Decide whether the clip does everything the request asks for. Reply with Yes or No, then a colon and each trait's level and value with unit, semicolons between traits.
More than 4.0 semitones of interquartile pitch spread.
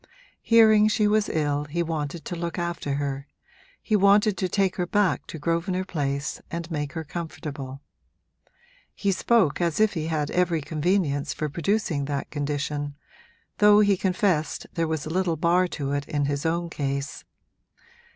Yes: average, 4.4 semitones